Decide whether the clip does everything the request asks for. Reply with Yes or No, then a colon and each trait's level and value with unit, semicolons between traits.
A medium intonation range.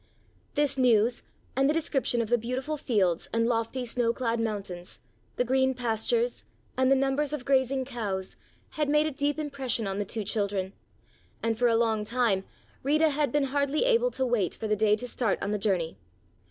Yes: average, 4.2 semitones